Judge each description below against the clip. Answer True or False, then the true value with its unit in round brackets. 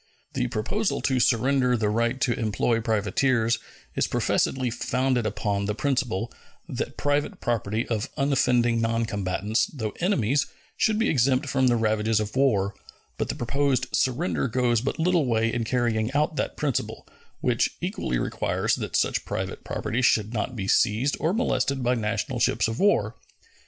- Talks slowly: False (155 wpm)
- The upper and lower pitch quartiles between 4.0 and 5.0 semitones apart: False (3.6 semitones)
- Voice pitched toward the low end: True (120 Hz)